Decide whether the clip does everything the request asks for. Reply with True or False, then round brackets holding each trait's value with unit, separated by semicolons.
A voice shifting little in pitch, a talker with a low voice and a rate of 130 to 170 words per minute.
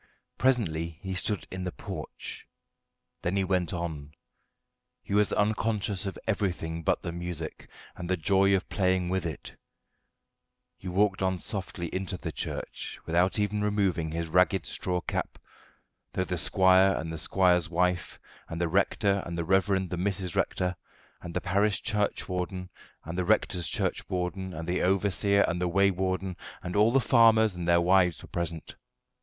True (2.2 semitones; 95 Hz; 160 wpm)